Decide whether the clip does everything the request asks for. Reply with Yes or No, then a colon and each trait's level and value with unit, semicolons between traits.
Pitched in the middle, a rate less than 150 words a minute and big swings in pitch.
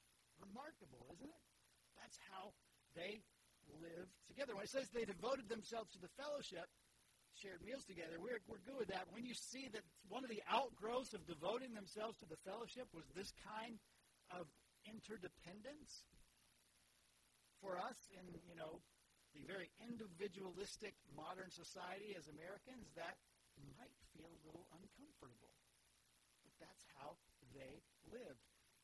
No: high, 195 Hz; average, 140 wpm; wide, 5.8 semitones